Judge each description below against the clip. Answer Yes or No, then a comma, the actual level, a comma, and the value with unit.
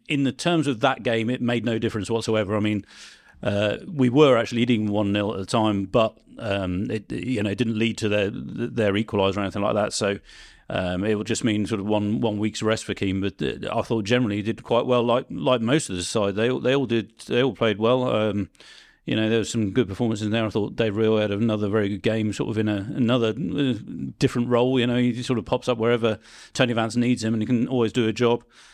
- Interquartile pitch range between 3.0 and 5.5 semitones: No, narrow, 2.5 semitones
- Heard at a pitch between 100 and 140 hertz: Yes, low, 115 Hz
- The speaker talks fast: Yes, fast, 250 wpm